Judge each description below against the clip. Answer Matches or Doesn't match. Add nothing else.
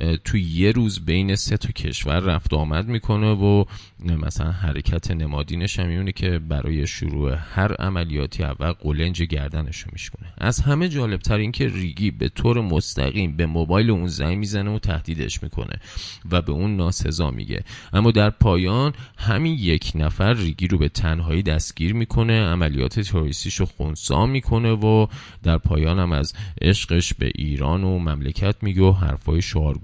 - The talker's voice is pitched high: Doesn't match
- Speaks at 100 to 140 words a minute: Doesn't match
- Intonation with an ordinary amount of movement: Matches